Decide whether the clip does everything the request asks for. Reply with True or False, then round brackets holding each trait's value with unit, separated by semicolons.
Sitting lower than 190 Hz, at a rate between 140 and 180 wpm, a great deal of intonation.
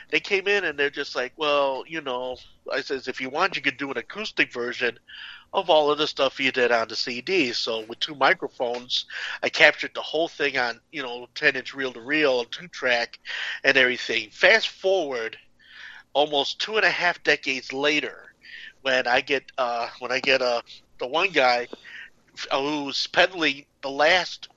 False (140 Hz; 175 wpm; 3.6 semitones)